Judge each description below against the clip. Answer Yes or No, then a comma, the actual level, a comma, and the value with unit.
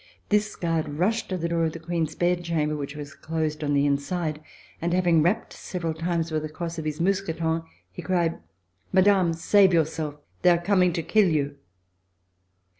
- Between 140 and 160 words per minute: No, average, 185 wpm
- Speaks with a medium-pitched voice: Yes, medium, 165 Hz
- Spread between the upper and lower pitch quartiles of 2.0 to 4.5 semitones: Yes, narrow, 2.4 semitones